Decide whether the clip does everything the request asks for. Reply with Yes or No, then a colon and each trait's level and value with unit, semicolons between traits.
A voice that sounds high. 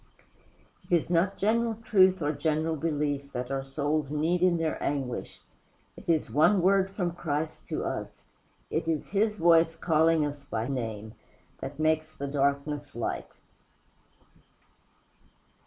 No: medium, 155 Hz